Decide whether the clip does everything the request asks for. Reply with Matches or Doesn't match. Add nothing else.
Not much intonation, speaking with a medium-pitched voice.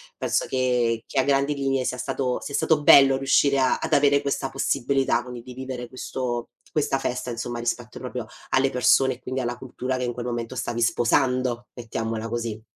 Doesn't match